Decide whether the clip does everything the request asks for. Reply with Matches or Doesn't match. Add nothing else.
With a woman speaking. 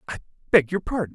Doesn't match